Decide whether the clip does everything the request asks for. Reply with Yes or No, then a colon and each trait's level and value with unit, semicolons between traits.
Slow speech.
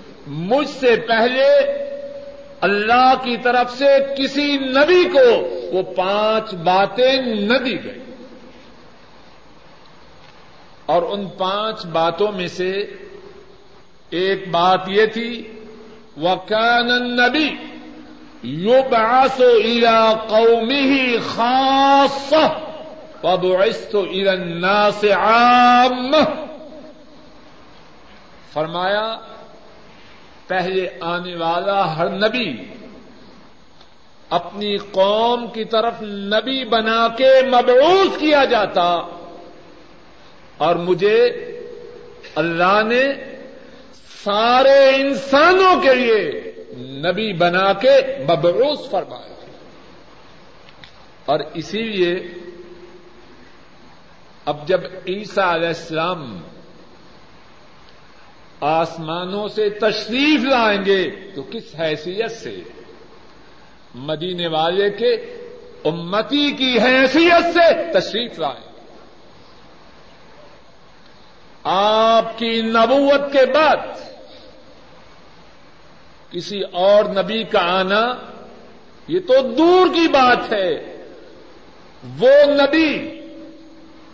Yes: slow, 80 wpm